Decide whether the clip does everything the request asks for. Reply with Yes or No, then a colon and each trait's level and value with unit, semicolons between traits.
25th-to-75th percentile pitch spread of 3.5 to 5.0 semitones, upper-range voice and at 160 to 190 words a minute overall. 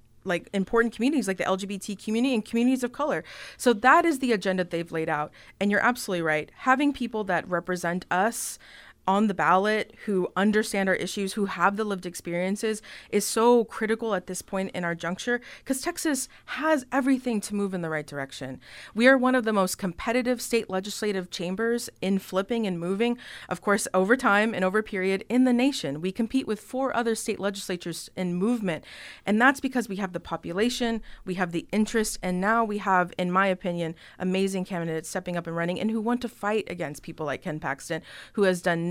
No: average, 4.4 semitones; high, 200 Hz; average, 200 wpm